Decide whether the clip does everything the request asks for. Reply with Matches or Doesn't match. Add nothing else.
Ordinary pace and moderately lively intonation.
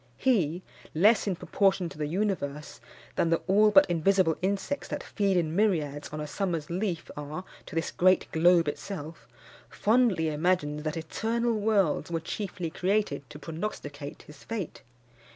Matches